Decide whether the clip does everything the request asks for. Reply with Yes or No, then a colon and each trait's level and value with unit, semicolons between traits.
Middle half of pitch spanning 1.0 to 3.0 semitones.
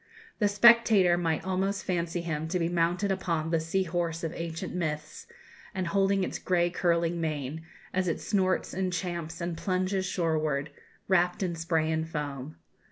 Yes: narrow, 2.4 semitones